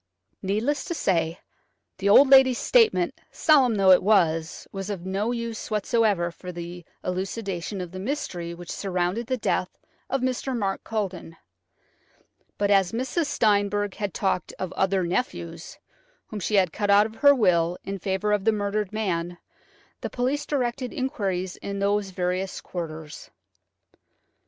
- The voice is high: Yes, high, 200 Hz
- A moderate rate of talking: Yes, average, 150 wpm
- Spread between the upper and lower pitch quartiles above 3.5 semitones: Yes, average, 4.1 semitones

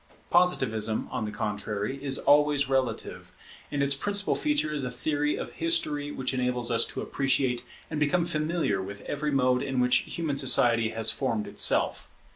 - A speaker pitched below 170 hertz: Yes, low, 135 Hz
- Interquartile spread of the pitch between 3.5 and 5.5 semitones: Yes, average, 3.9 semitones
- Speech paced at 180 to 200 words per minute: No, average, 165 wpm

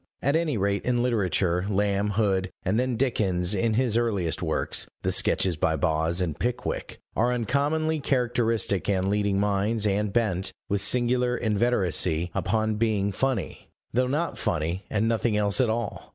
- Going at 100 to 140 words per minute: No, average, 155 wpm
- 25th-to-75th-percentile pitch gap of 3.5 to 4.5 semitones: Yes, average, 4.0 semitones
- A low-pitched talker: Yes, low, 105 Hz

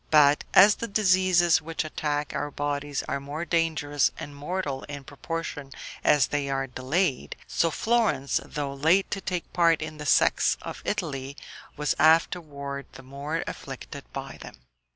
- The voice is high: No, medium, 150 Hz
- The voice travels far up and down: No, average, 3.1 semitones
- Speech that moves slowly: No, average, 150 wpm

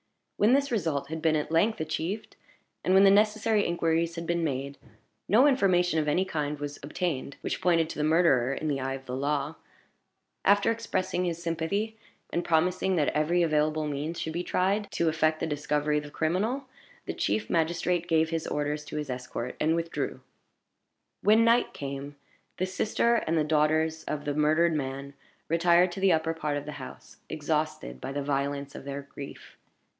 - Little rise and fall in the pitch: No, average, 3.4 semitones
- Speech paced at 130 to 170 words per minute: No, average, 185 wpm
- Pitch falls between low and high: Yes, medium, 160 Hz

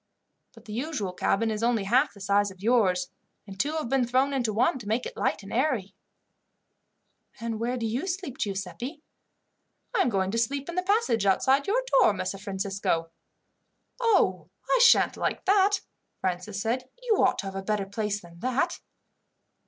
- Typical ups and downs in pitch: No, wide, 5.9 semitones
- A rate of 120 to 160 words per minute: No, average, 185 wpm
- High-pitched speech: Yes, high, 230 Hz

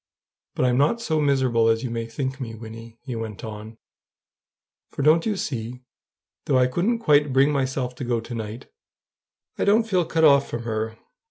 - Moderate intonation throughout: Yes, average, 4.4 semitones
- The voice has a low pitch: Yes, low, 130 Hz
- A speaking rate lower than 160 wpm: No, average, 185 wpm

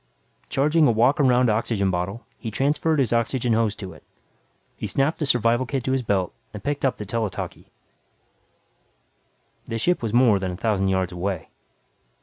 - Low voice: Yes, low, 115 Hz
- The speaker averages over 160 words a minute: Yes, average, 175 wpm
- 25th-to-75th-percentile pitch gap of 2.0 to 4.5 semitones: No, average, 5.0 semitones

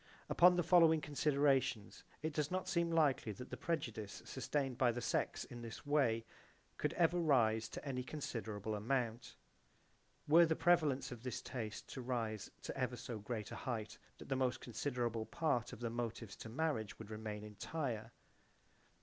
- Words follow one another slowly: No, average, 165 wpm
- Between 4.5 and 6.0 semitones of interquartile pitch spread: Yes, average, 5.1 semitones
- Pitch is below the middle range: Yes, low, 125 Hz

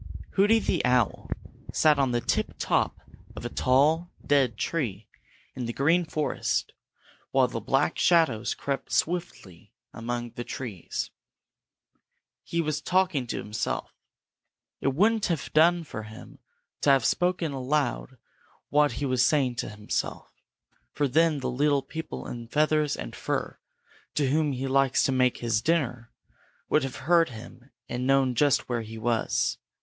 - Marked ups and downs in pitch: No, average, 4.2 semitones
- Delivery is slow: No, average, 150 wpm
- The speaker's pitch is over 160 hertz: No, low, 135 Hz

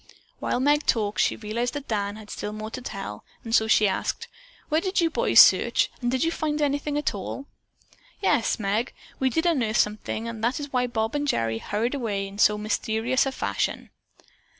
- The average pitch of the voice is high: Yes, high, 230 Hz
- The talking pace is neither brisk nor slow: Yes, average, 195 wpm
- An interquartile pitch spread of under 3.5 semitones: No, average, 5.1 semitones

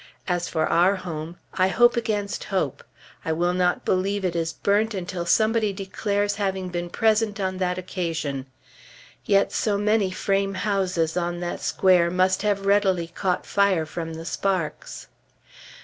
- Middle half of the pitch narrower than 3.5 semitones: Yes, narrow, 2.6 semitones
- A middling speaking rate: Yes, average, 150 wpm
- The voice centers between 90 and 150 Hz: No, medium, 185 Hz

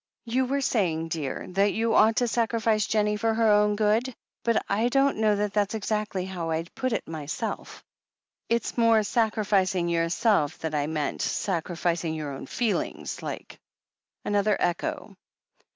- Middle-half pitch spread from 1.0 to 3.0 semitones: No, average, 4.8 semitones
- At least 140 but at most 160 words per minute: Yes, average, 155 wpm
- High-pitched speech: Yes, high, 210 Hz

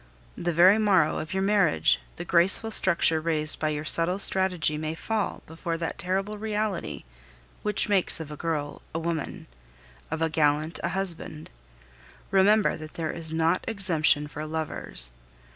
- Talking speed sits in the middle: Yes, average, 155 wpm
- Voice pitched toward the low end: No, medium, 165 Hz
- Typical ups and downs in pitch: Yes, average, 3.6 semitones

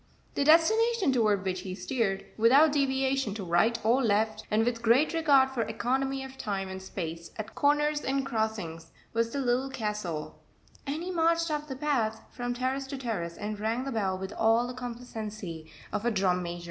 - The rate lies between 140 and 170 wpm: No, average, 185 wpm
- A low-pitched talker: No, high, 235 Hz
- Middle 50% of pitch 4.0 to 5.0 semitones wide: Yes, average, 4.7 semitones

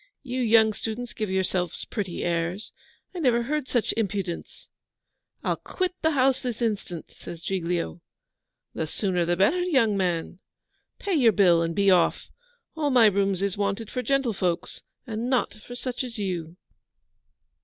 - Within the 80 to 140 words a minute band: No, average, 155 wpm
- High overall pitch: Yes, high, 210 Hz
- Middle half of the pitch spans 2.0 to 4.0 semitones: No, wide, 5.4 semitones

